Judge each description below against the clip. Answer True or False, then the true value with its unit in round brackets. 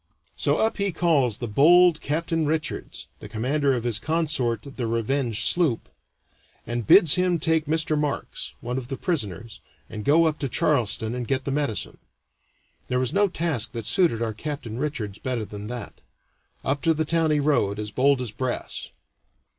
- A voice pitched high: False (135 Hz)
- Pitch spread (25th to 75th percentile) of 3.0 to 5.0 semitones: False (5.4 semitones)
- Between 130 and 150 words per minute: False (175 wpm)